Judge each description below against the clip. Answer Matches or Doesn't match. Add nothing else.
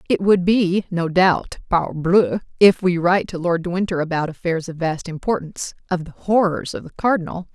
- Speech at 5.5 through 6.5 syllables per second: Doesn't match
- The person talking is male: Doesn't match